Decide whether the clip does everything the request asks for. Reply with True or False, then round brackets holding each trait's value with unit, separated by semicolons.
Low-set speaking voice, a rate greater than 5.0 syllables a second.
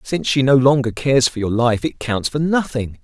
True (130 Hz; 5.5 syllables/s)